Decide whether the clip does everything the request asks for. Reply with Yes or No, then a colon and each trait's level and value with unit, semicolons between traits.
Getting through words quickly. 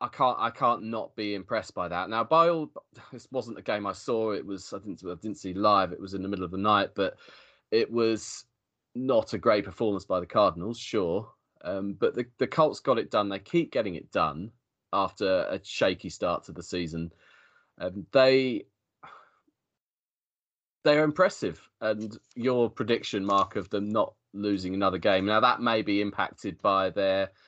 No: average, 190 wpm